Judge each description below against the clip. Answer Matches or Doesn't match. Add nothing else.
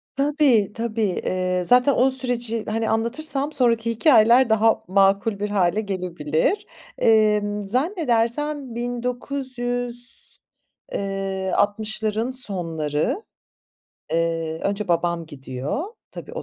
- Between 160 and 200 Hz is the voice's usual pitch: Doesn't match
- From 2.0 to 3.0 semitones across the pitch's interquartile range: Doesn't match